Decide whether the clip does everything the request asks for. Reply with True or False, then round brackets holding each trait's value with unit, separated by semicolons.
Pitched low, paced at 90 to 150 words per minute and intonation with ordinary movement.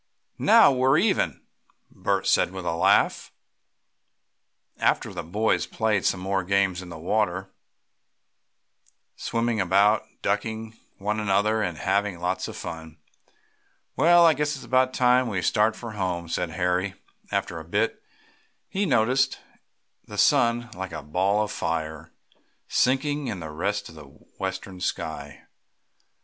True (100 Hz; 135 wpm; 4.7 semitones)